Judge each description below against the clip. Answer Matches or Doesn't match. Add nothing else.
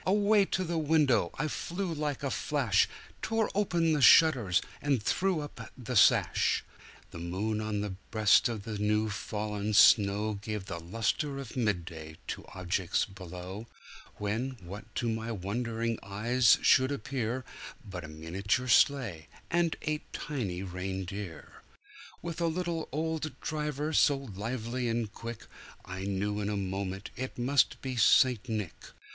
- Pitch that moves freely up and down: Matches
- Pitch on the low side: Matches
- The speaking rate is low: Doesn't match